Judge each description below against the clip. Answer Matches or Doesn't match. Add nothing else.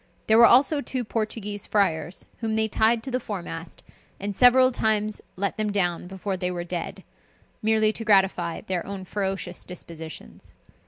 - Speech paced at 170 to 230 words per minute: Doesn't match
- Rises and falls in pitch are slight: Doesn't match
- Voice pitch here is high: Matches